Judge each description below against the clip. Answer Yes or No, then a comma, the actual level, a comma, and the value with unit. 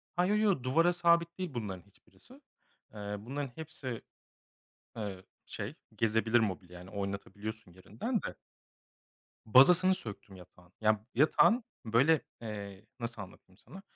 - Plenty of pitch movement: Yes, wide, 8.3 semitones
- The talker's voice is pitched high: No, low, 110 Hz